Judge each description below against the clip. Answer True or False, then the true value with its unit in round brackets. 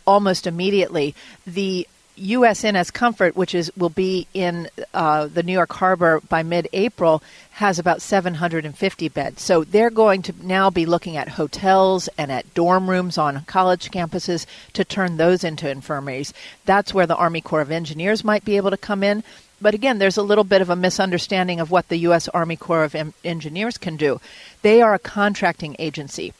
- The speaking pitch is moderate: True (180 Hz)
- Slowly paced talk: False (185 wpm)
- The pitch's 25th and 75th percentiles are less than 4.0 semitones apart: True (3.0 semitones)